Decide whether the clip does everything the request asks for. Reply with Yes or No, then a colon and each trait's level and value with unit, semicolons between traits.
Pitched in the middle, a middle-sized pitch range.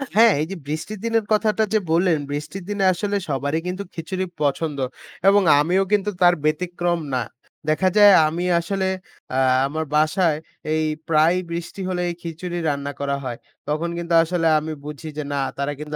Yes: medium, 170 Hz; average, 3.6 semitones